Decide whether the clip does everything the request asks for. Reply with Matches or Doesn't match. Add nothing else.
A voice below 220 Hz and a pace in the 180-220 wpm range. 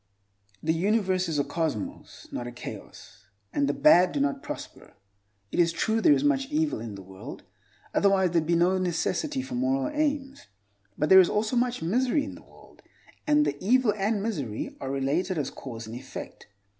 Matches